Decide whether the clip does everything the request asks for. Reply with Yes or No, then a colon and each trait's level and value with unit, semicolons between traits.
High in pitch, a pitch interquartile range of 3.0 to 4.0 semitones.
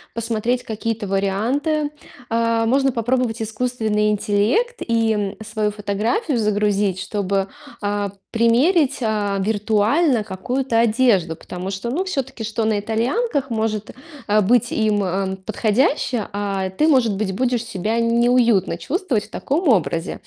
Yes: high, 220 Hz; average, 3.4 semitones